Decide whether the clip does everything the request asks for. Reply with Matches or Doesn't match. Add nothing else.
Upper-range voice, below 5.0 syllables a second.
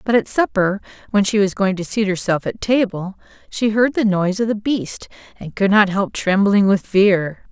Matches